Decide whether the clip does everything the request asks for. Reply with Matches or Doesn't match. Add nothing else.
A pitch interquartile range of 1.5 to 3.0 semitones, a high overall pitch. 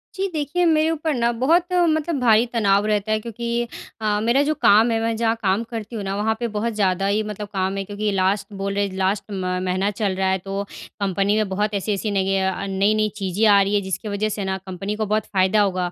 Matches